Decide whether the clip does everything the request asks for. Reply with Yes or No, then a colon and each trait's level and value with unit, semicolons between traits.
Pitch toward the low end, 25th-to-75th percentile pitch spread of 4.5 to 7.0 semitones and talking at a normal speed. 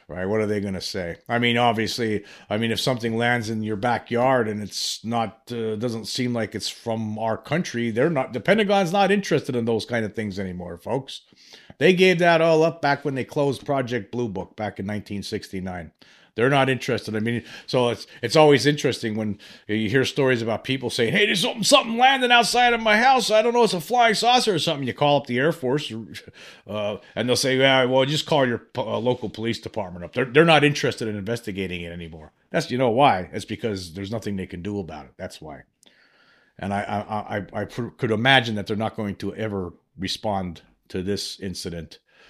No: low, 115 Hz; average, 5.0 semitones; fast, 215 wpm